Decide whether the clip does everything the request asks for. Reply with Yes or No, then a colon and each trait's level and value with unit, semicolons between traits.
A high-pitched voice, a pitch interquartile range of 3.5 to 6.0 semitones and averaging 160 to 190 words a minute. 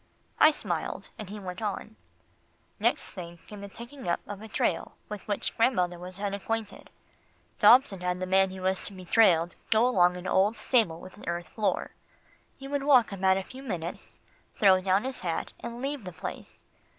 Yes: high, 195 Hz; average, 3.8 semitones; average, 185 wpm